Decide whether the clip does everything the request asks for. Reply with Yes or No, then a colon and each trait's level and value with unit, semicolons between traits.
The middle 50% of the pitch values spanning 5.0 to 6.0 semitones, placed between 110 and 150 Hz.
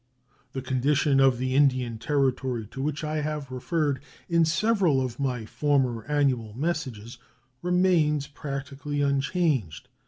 No: average, 2.9 semitones; medium, 140 Hz